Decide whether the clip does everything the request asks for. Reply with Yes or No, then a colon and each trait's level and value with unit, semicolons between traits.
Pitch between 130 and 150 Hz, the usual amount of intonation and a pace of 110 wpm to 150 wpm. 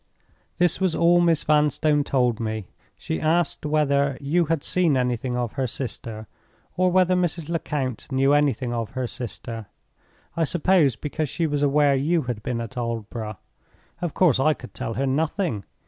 No: medium, 140 Hz; average, 4.8 semitones; average, 160 wpm